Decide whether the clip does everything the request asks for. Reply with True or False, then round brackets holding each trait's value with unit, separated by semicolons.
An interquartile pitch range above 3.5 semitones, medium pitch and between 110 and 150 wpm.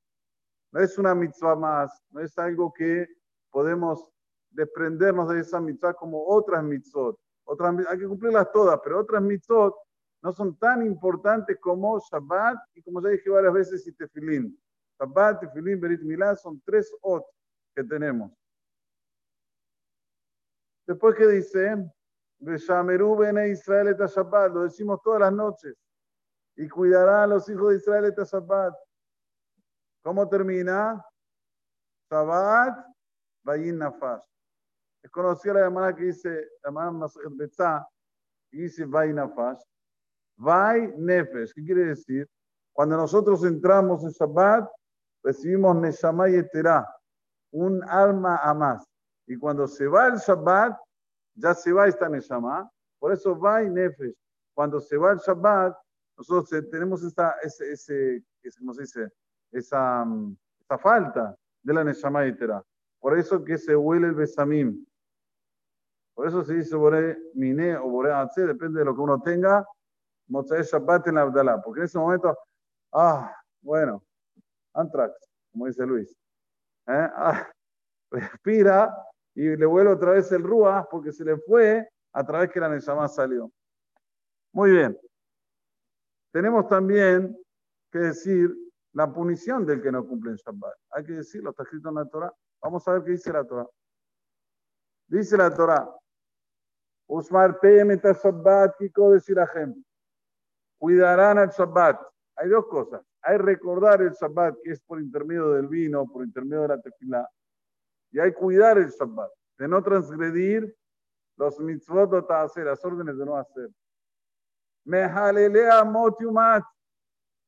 True (4.7 semitones; 175 Hz; 135 wpm)